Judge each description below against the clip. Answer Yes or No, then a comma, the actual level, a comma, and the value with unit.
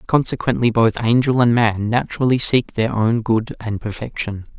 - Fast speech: No, average, 155 wpm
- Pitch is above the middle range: No, low, 115 Hz